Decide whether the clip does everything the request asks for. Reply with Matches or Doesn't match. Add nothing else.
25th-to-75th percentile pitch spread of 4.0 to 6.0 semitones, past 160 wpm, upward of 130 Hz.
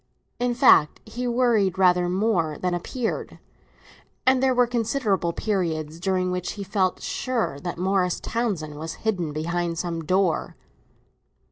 Doesn't match